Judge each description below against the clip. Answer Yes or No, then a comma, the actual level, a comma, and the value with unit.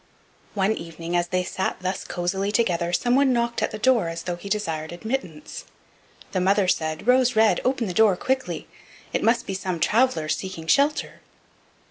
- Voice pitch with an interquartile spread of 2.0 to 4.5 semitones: No, average, 5.3 semitones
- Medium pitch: No, high, 195 Hz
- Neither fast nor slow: Yes, average, 170 wpm